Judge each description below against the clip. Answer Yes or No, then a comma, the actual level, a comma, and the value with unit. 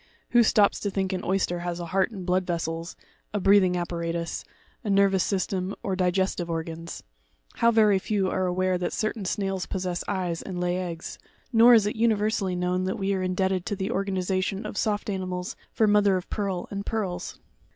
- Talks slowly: No, average, 190 wpm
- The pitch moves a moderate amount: No, narrow, 2.0 semitones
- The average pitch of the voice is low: No, high, 190 Hz